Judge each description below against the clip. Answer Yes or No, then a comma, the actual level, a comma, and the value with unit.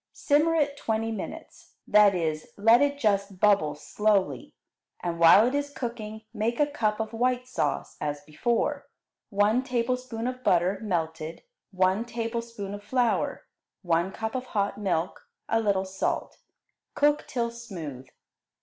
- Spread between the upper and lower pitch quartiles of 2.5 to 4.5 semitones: Yes, average, 4.1 semitones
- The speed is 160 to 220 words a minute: No, average, 140 wpm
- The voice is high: Yes, high, 215 Hz